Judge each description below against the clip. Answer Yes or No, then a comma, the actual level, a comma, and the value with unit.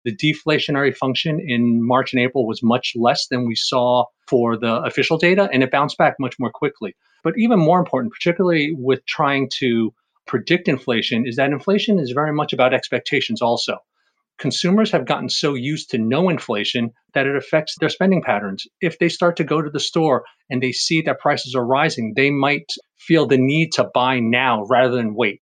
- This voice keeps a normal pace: Yes, average, 195 wpm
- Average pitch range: Yes, average, 4.7 semitones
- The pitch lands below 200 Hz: Yes, low, 135 Hz